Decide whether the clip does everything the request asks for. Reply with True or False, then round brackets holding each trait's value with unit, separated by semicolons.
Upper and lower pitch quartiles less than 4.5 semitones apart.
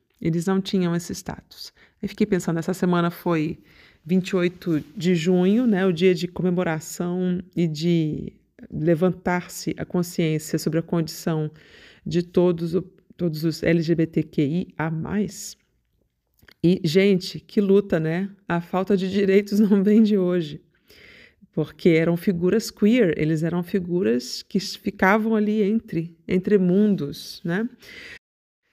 True (2.9 semitones)